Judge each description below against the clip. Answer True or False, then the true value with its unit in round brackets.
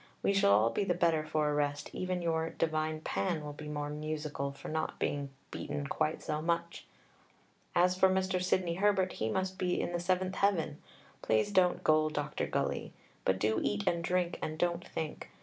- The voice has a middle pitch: True (160 Hz)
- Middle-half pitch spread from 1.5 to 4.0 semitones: True (3.4 semitones)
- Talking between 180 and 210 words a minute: True (190 wpm)